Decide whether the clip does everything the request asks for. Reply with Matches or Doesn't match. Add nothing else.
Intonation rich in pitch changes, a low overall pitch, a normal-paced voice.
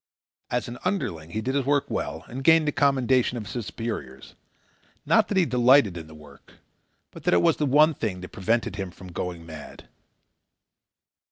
Matches